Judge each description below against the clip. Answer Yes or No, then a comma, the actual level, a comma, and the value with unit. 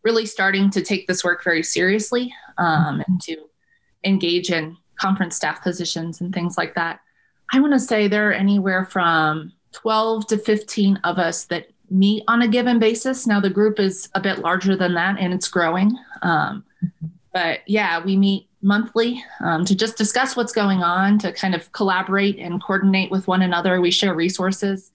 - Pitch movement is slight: No, average, 3.2 semitones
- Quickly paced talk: No, average, 185 wpm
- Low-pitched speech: No, high, 195 Hz